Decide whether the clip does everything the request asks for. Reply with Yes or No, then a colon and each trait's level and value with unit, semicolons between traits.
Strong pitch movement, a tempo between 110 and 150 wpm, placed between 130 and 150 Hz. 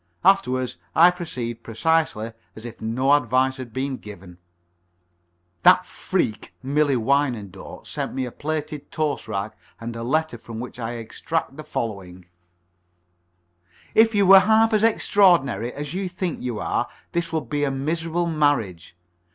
Yes: wide, 5.9 semitones; average, 145 wpm; low, 135 Hz